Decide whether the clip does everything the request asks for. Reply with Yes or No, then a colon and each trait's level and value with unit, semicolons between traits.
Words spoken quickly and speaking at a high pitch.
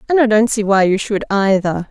Yes: fast, 250 wpm; high, 210 Hz